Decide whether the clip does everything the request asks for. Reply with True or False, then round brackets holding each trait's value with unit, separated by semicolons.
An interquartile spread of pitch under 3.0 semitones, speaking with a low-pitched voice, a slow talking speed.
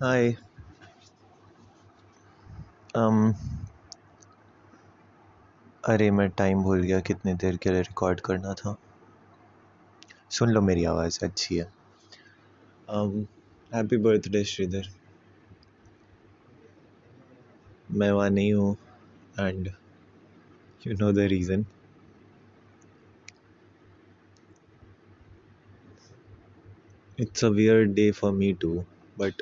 True (2.5 semitones; 105 Hz; 80 wpm)